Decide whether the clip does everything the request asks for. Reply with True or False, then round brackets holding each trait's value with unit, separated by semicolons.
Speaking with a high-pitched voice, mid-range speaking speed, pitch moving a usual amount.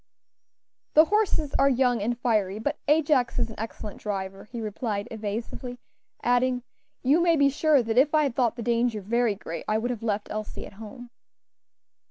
True (240 Hz; 180 wpm; 4.0 semitones)